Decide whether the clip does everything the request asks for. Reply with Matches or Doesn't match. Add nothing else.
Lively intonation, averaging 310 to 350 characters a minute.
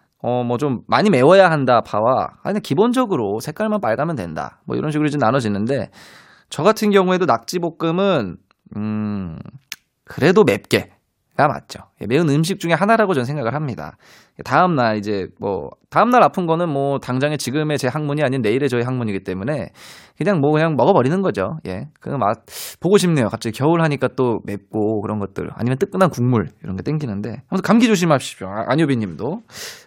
Doesn't match